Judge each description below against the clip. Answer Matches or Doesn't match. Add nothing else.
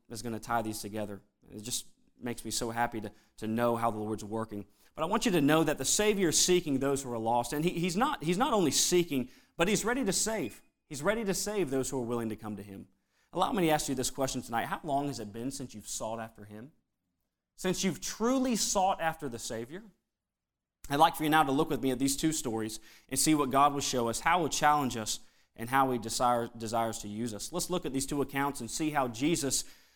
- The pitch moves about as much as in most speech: Doesn't match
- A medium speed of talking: Doesn't match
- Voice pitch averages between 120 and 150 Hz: Matches